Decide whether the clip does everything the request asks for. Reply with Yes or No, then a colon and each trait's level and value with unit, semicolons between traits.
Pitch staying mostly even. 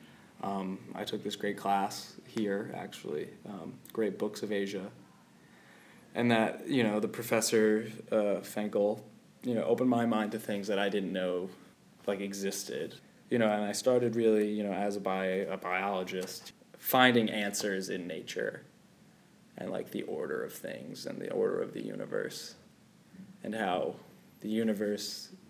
No: average, 3.7 semitones